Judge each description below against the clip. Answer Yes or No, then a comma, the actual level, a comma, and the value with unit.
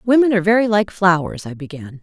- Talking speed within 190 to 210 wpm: Yes, fast, 205 wpm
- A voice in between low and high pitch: No, high, 195 Hz